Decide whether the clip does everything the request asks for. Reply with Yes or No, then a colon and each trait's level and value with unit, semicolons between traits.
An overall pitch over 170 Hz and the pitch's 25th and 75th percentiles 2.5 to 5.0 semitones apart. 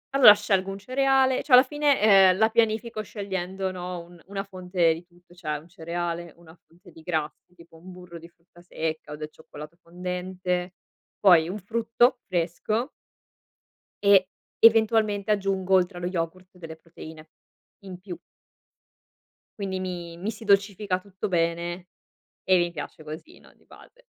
Yes: medium, 185 Hz; average, 2.9 semitones